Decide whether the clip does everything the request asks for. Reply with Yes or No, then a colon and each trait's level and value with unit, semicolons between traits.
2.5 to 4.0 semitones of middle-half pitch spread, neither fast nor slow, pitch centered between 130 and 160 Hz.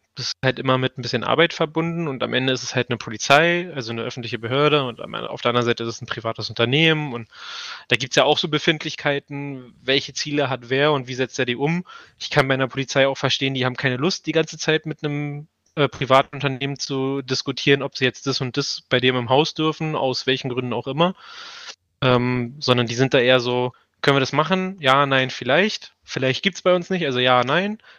No: average, 3.2 semitones; fast, 230 wpm; low, 135 Hz